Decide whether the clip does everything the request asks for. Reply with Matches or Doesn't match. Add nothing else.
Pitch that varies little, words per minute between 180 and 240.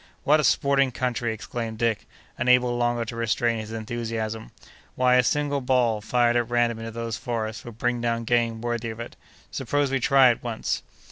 Matches